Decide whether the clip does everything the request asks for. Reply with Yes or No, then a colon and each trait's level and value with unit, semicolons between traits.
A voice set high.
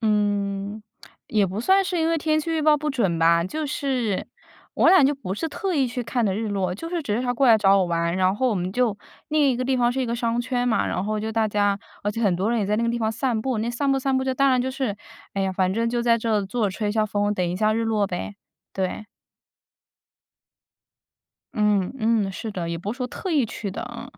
Yes: high, 225 Hz